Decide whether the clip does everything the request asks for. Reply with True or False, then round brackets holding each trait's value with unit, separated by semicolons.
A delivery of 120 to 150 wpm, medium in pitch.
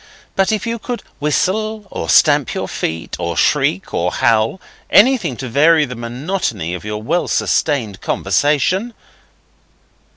True (140 wpm; 145 Hz)